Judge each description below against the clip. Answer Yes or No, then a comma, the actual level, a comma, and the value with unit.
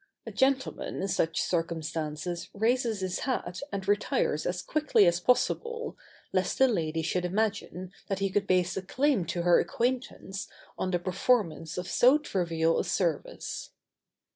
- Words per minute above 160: No, average, 150 wpm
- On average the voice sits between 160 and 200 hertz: Yes, medium, 185 Hz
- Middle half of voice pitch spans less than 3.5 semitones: No, average, 5.2 semitones